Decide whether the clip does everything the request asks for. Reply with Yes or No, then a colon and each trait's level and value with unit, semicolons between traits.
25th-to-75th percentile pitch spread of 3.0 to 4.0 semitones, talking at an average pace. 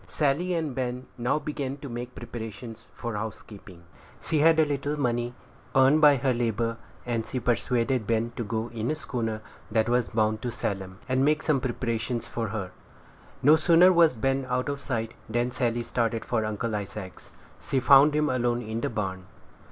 Yes: average, 3.4 semitones; average, 180 wpm